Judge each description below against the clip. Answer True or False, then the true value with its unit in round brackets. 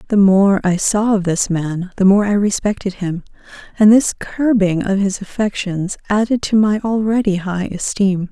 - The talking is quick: False (175 wpm)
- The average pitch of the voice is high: True (200 Hz)